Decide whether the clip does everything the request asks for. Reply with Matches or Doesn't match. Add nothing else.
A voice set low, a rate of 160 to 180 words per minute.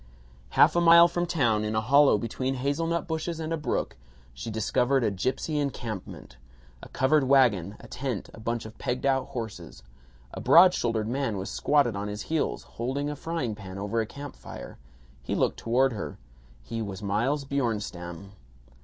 Matches